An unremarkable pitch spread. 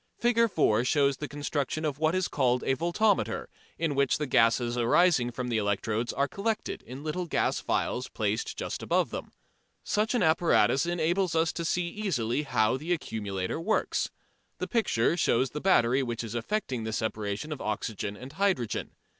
No: wide, 6.6 semitones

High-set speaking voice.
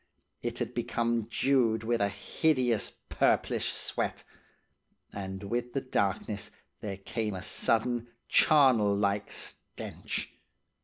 No: low, 110 Hz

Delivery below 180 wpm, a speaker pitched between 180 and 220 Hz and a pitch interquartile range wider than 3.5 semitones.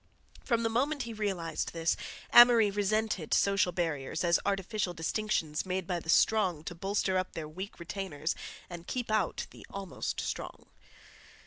Yes: average, 150 wpm; high, 190 Hz; average, 4.0 semitones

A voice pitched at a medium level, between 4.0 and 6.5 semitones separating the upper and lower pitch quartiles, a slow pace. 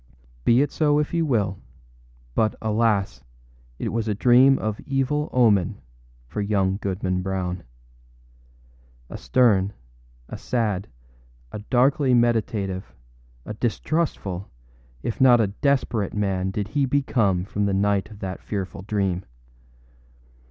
No: low, 105 Hz; average, 4.4 semitones; slow, 125 wpm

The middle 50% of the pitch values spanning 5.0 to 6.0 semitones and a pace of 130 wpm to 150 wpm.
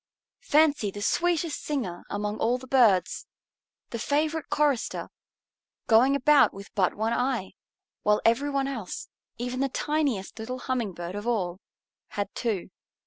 Yes: average, 5.3 semitones; average, 140 wpm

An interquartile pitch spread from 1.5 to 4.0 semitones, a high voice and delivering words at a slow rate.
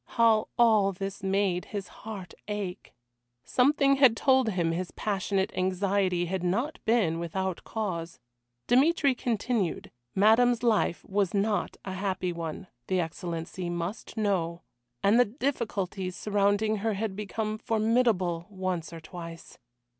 Yes: average, 3.6 semitones; high, 200 Hz; slow, 130 wpm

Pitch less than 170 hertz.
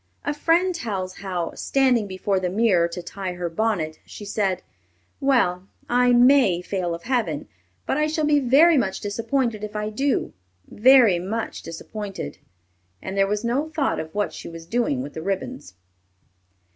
No: high, 210 Hz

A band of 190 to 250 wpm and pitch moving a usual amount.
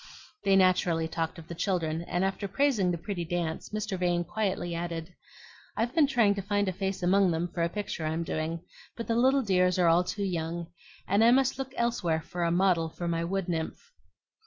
Yes: fast, 205 wpm; average, 3.3 semitones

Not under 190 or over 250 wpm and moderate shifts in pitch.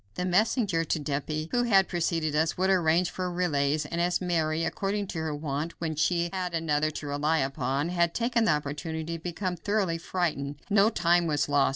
Yes: average, 195 wpm; average, 3.0 semitones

